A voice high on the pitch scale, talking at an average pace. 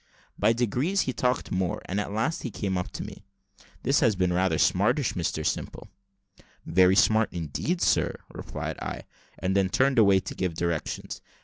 No: low, 100 Hz; average, 170 wpm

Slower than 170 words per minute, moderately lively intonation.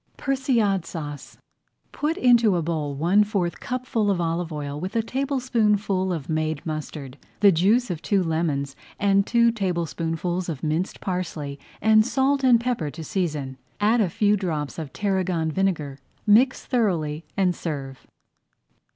No: average, 140 wpm; wide, 5.7 semitones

